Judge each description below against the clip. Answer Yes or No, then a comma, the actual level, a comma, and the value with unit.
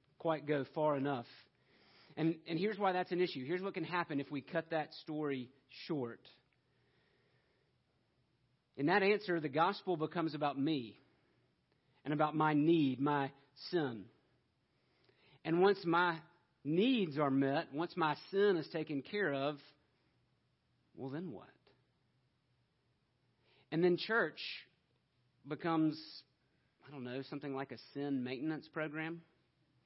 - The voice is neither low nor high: Yes, medium, 150 Hz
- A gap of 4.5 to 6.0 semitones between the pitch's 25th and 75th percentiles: No, average, 3.5 semitones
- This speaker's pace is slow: Yes, slow, 130 wpm